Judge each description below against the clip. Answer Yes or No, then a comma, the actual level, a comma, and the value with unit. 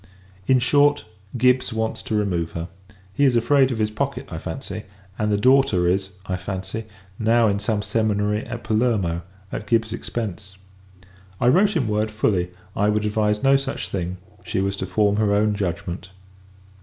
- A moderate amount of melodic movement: Yes, average, 3.2 semitones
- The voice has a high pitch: No, low, 105 Hz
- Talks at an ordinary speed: Yes, average, 170 wpm